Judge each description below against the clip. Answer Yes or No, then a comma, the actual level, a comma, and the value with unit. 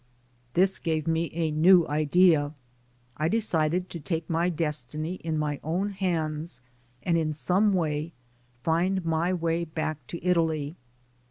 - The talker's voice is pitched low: No, medium, 165 Hz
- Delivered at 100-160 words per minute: Yes, average, 140 wpm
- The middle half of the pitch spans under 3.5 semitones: Yes, narrow, 2.4 semitones